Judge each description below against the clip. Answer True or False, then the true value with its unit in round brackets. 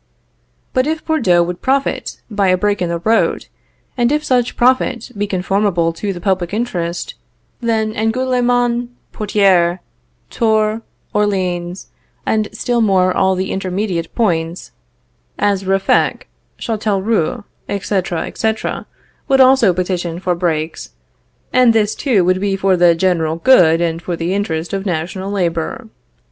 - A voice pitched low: False (195 Hz)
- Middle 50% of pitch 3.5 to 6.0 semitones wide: True (4.1 semitones)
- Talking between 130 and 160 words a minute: True (135 wpm)